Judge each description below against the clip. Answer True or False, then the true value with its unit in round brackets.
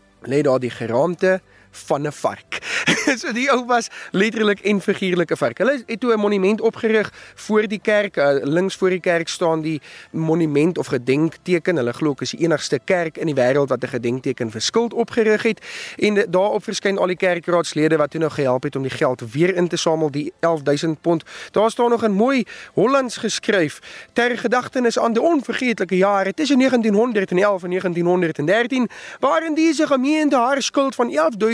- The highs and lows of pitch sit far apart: True (6.2 semitones)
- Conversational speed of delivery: True (180 wpm)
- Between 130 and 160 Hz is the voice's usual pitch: False (190 Hz)